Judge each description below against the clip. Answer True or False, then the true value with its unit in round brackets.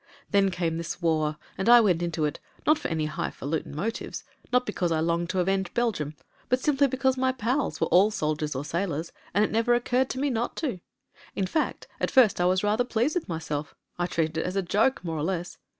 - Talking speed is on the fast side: True (230 wpm)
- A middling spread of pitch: False (6.8 semitones)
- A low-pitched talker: False (190 Hz)